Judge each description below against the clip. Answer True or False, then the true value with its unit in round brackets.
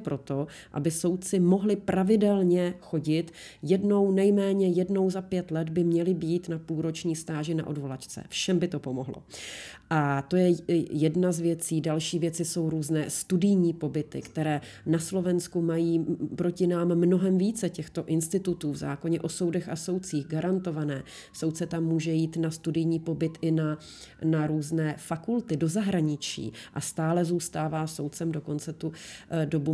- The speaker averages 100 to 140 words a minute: False (150 wpm)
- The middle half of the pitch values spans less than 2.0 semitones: False (2.3 semitones)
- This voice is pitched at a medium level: True (165 Hz)